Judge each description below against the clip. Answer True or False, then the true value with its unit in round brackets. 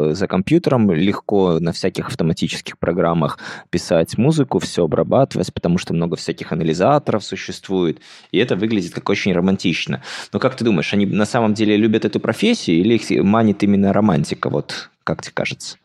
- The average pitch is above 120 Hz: False (100 Hz)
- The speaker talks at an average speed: False (165 wpm)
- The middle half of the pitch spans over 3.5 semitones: True (4.1 semitones)